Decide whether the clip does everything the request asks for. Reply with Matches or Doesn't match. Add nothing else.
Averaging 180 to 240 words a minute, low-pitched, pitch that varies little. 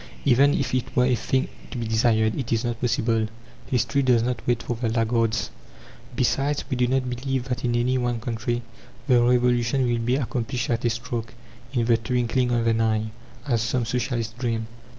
Matches